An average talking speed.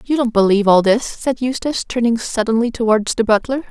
Yes: average, 195 wpm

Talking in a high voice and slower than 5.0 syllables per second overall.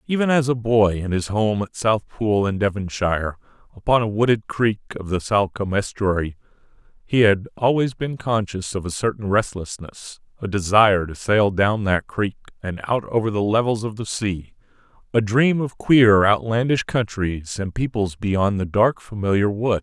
No: low, 105 Hz; 4.8 syllables/s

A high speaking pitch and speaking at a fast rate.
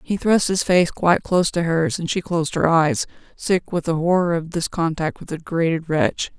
No: medium, 165 Hz; fast, 225 wpm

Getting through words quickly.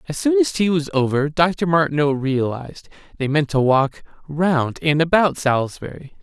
No: average, 165 wpm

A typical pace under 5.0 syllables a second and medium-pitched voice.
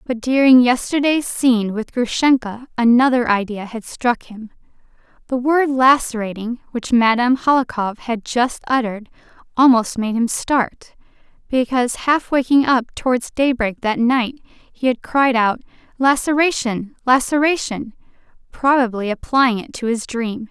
No: 4.4 syllables/s; high, 245 Hz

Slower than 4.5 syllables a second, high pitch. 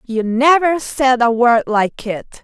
Yes: 3.6 syllables/s; very high, 250 Hz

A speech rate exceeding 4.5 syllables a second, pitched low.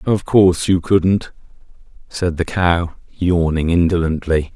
No: 3.9 syllables/s; very low, 85 Hz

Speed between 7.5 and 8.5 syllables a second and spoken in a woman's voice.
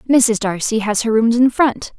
No: 4.6 syllables/s; female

